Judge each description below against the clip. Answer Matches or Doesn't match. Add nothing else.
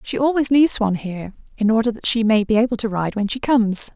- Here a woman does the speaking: Matches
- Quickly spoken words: Matches